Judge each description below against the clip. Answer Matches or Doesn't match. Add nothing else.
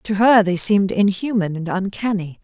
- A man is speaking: Doesn't match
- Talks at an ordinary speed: Matches